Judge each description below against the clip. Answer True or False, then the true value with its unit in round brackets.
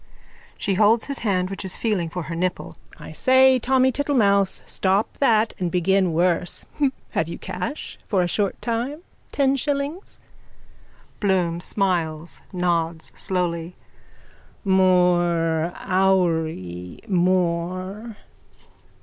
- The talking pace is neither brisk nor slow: False (110 wpm)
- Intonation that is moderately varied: True (4.1 semitones)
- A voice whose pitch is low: False (185 Hz)